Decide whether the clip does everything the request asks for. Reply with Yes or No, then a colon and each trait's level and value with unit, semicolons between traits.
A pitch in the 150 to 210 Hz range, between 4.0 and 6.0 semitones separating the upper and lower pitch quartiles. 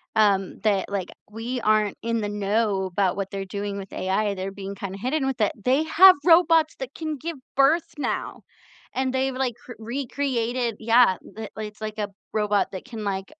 No: high, 220 Hz; average, 4.6 semitones